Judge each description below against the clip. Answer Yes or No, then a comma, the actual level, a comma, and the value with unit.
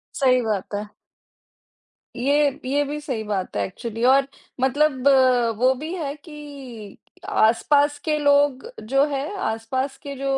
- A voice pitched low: No, very high, 270 Hz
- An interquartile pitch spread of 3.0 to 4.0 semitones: Yes, average, 3.5 semitones